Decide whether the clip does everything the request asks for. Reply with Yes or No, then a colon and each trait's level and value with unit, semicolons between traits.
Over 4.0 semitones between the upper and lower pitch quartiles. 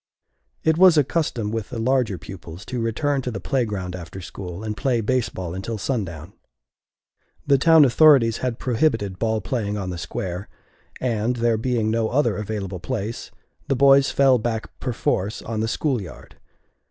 Yes: average, 4.4 semitones